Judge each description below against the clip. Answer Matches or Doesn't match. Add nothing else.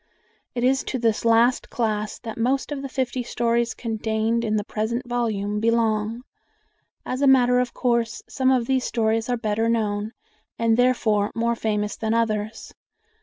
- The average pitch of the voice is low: Doesn't match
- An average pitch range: Doesn't match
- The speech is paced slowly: Doesn't match